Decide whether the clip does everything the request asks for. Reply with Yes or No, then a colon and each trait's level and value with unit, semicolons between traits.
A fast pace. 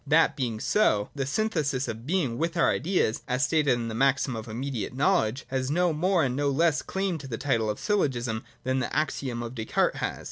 Yes: fast, 210 wpm